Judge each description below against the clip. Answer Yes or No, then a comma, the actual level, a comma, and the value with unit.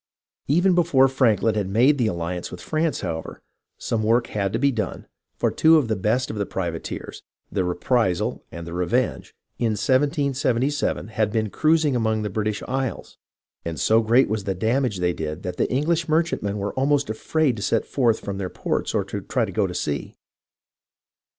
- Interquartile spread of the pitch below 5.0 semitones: No, wide, 5.4 semitones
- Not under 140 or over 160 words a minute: No, average, 185 wpm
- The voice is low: Yes, low, 110 Hz